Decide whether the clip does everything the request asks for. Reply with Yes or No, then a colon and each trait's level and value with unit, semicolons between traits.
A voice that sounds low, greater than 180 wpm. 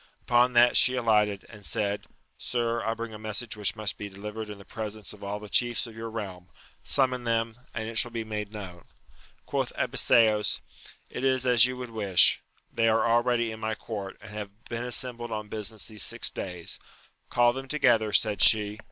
Yes: low, 110 Hz; average, 195 wpm